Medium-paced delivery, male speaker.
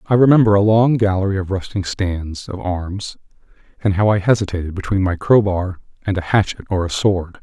Yes: average, 185 wpm; male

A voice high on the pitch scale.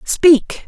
Yes: very high, 295 Hz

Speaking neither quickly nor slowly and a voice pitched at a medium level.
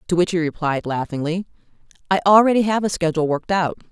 Yes: average, 185 wpm; medium, 175 Hz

